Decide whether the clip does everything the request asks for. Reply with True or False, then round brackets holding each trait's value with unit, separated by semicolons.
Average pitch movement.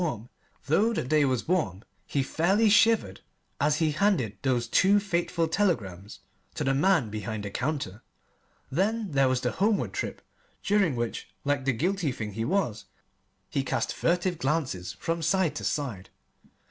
False (7.9 semitones)